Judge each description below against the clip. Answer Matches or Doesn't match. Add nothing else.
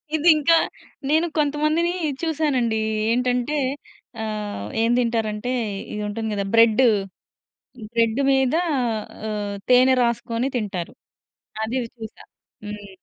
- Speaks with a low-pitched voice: Doesn't match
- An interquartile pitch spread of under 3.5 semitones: Doesn't match